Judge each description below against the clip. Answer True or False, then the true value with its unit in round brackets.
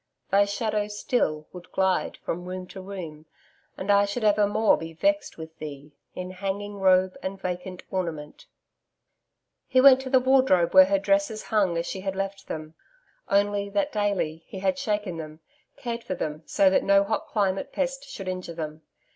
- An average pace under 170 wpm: False (175 wpm)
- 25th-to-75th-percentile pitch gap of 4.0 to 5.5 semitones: False (2.6 semitones)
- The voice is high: True (195 Hz)